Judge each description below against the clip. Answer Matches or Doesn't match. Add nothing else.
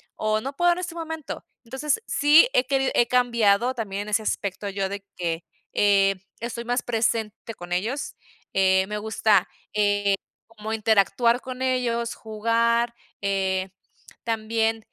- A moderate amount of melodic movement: Matches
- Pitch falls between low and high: Doesn't match